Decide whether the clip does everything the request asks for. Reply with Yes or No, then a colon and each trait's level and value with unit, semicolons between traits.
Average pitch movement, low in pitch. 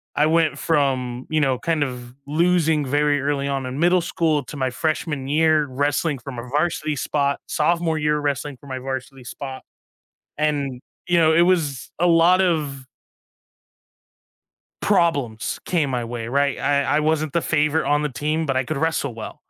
No: average, 3.0 semitones; medium, 145 Hz